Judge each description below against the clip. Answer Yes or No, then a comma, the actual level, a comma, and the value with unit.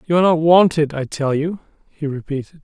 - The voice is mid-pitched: Yes, medium, 155 Hz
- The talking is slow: No, fast, 205 wpm